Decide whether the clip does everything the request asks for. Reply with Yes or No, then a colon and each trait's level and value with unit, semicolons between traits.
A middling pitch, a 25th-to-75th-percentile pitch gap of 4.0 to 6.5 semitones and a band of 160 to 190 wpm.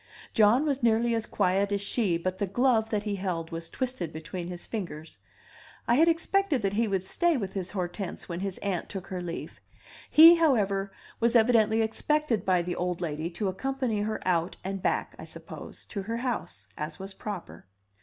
No: high, 200 Hz; average, 4.6 semitones; average, 185 wpm